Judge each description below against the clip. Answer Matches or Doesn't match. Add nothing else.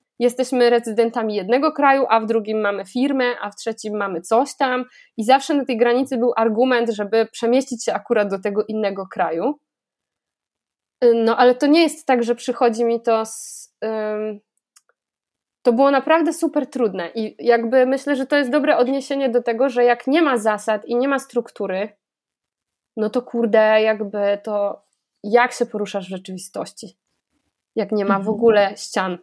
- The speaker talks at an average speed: Doesn't match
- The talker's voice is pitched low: Doesn't match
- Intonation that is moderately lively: Matches